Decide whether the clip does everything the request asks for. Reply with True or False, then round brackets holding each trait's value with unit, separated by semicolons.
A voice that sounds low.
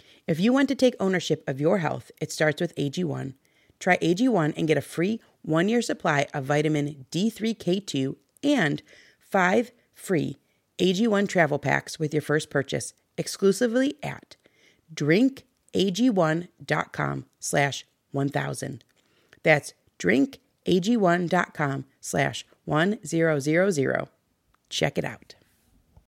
False (165 Hz)